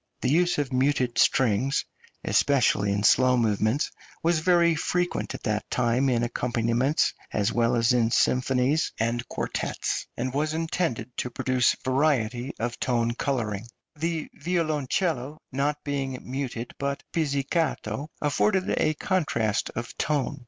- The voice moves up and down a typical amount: Yes, average, 4.2 semitones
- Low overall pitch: Yes, low, 130 Hz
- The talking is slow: Yes, slow, 130 wpm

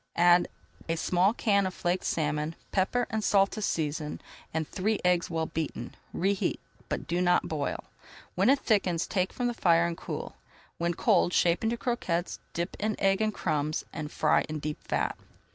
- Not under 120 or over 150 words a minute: No, average, 180 wpm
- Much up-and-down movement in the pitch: No, average, 3.8 semitones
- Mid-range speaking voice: Yes, medium, 175 Hz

